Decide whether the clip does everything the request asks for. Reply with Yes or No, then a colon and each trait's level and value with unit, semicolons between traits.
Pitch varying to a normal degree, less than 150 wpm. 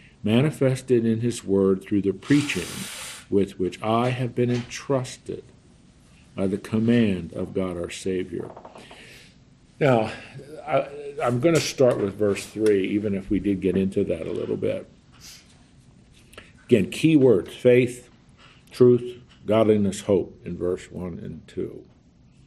Yes: average, 4.4 semitones; slow, 135 wpm